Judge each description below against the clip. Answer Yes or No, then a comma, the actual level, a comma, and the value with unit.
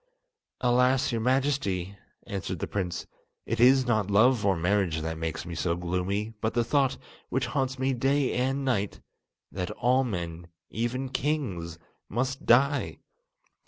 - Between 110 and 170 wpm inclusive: Yes, average, 145 wpm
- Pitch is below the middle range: Yes, low, 115 Hz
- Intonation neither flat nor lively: No, wide, 6.2 semitones